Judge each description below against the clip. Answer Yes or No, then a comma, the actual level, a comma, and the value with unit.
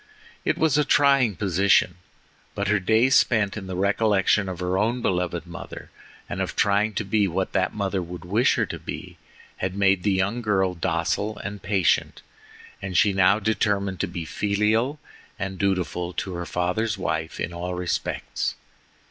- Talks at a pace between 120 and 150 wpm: No, average, 170 wpm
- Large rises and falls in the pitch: No, average, 2.7 semitones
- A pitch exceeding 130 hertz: No, low, 100 Hz